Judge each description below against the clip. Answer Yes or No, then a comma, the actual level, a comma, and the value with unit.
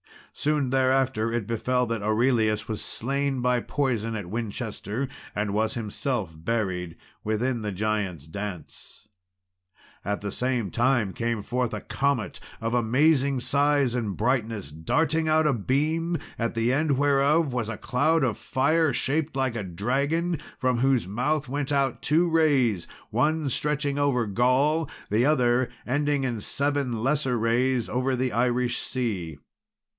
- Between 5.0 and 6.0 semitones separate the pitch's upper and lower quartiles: No, average, 4.2 semitones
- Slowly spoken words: No, average, 145 wpm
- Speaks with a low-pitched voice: Yes, low, 125 Hz